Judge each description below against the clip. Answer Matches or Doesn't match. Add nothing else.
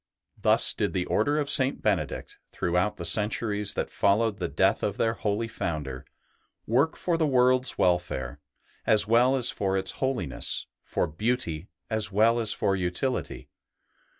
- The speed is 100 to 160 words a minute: Matches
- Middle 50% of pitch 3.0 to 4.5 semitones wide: Doesn't match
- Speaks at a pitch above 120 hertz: Doesn't match